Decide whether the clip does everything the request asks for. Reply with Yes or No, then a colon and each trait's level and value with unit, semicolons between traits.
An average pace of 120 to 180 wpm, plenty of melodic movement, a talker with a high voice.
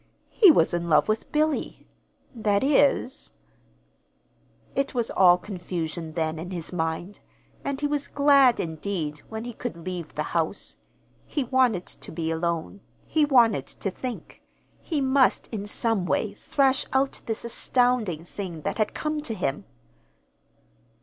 Yes: average, 145 wpm; wide, 7.4 semitones; high, 215 Hz